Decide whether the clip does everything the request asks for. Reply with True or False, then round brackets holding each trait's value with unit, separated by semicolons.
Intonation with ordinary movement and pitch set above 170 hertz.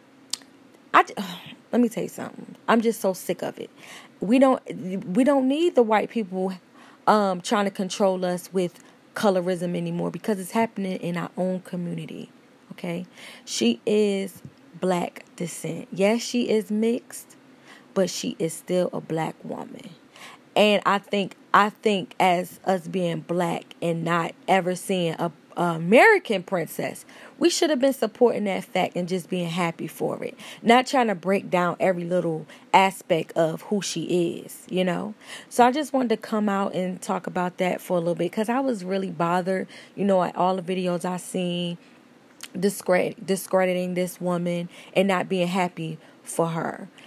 True (4.8 semitones; 190 Hz)